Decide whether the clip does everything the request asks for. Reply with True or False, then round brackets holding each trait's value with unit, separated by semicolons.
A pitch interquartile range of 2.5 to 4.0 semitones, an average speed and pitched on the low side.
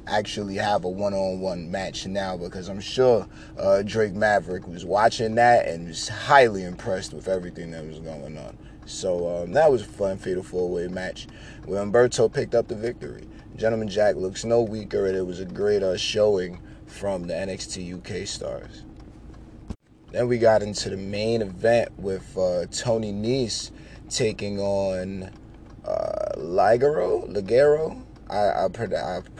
True (3.3 semitones; 165 wpm; 100 Hz)